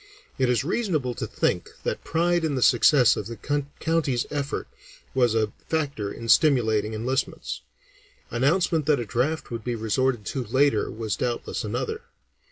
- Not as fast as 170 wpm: Yes, average, 155 wpm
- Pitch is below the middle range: Yes, low, 125 Hz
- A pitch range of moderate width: Yes, average, 4.5 semitones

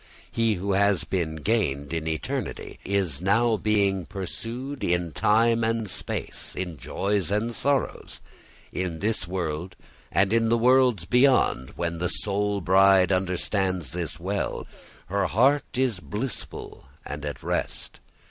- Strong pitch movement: No, average, 4.5 semitones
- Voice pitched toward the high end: No, low, 100 Hz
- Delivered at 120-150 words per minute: Yes, slow, 135 wpm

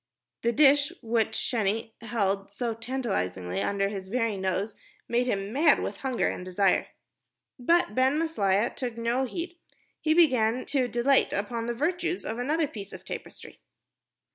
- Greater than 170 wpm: No, average, 150 wpm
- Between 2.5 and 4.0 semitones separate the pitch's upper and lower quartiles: No, average, 4.9 semitones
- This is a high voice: Yes, high, 235 Hz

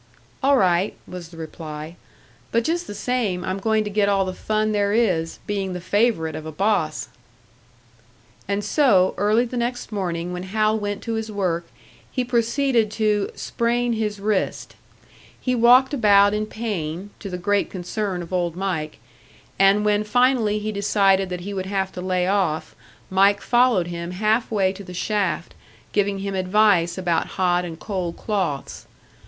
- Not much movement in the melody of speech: No, average, 3.1 semitones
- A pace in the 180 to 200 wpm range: No, average, 170 wpm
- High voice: Yes, high, 200 Hz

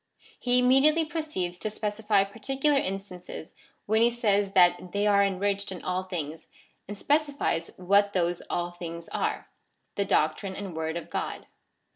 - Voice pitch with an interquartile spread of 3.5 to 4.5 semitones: Yes, average, 4.0 semitones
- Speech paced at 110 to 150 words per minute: No, average, 160 wpm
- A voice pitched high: Yes, high, 200 Hz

